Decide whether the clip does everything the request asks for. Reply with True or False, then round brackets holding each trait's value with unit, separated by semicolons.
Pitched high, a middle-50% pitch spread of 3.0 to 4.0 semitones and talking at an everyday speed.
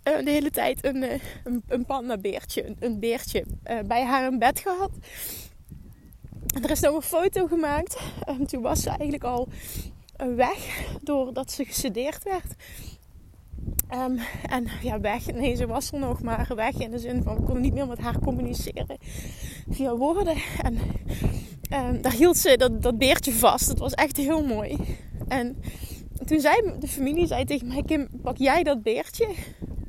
True (275 Hz; 3.5 semitones; 170 wpm)